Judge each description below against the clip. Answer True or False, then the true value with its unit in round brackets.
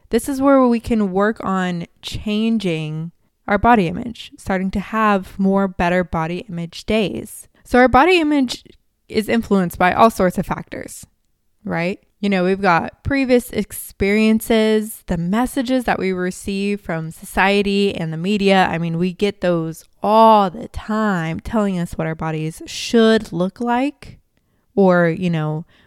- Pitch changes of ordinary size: True (3.8 semitones)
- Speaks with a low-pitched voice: False (200 Hz)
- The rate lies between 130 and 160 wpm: True (155 wpm)